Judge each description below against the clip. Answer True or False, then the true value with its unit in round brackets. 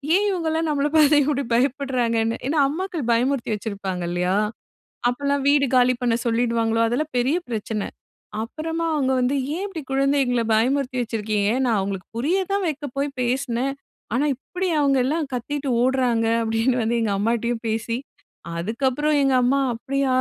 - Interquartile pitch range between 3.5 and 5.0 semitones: True (3.8 semitones)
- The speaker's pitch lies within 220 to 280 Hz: True (255 Hz)